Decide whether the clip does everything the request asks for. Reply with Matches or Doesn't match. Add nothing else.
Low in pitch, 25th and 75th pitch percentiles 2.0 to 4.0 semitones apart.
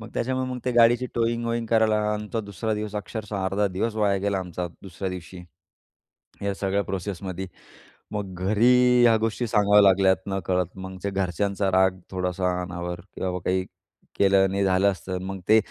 Matches